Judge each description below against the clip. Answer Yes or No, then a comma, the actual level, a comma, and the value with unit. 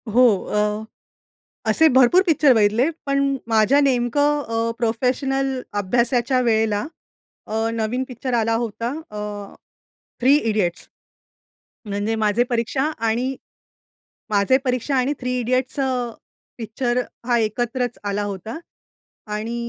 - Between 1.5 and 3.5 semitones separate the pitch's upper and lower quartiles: Yes, average, 3.1 semitones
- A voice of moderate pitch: No, high, 240 Hz